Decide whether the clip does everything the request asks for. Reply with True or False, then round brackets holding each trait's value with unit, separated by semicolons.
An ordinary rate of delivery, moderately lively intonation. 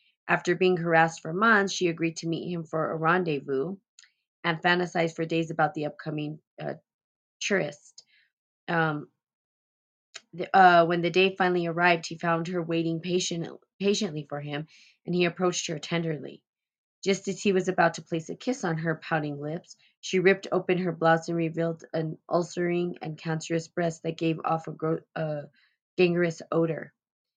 False (165 wpm; 1.7 semitones)